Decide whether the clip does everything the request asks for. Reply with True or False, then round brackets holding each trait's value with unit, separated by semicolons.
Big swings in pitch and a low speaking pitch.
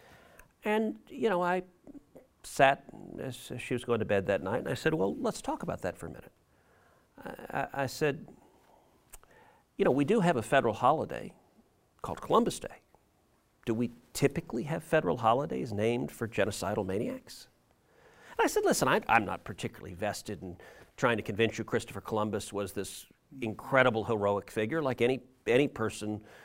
True (6.1 semitones; 120 Hz)